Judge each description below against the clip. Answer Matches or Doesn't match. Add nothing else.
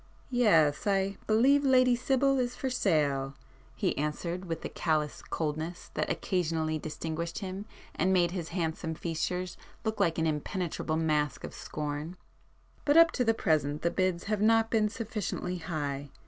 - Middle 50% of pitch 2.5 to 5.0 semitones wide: Doesn't match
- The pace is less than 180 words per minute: Matches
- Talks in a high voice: Doesn't match